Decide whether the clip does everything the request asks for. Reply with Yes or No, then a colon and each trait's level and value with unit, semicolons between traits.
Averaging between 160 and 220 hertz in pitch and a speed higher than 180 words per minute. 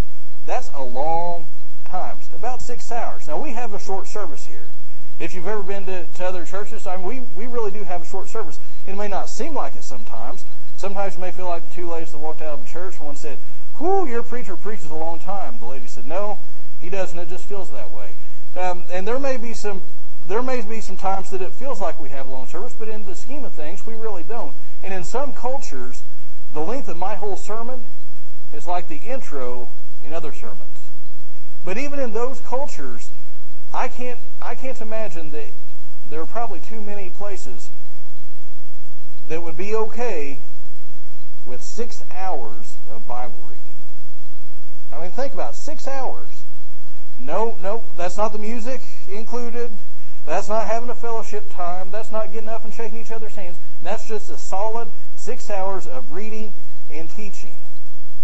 Yes: high, 190 Hz; average, 190 wpm